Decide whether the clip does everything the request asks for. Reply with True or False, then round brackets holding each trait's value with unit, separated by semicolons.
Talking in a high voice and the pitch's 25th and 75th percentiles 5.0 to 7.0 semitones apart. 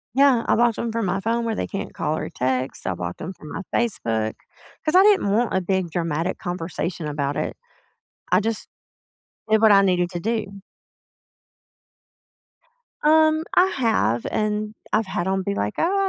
True (195 Hz; 5.6 semitones)